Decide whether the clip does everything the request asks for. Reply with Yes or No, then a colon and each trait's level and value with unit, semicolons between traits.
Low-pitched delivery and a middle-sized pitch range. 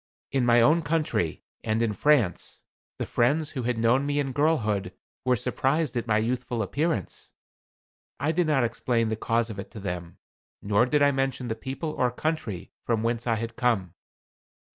Yes: low, 120 Hz; average, 4.3 semitones